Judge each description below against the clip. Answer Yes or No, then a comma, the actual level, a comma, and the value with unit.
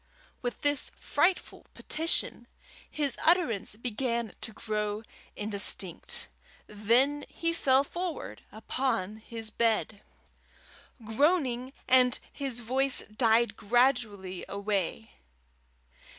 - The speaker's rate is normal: No, slow, 90 wpm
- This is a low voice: No, high, 235 Hz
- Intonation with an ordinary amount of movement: Yes, average, 4.2 semitones